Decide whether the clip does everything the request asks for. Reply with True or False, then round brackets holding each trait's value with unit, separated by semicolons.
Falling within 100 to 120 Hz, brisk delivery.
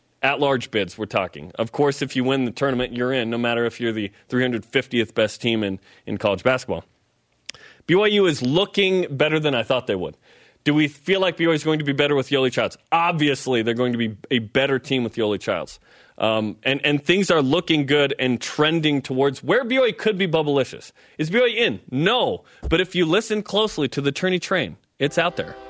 False (140 Hz; 210 wpm)